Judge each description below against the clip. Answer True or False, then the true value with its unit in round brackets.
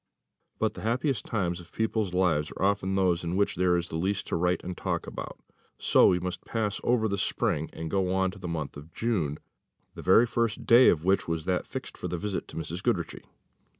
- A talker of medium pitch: False (90 Hz)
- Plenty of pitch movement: False (3.0 semitones)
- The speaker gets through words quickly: True (215 wpm)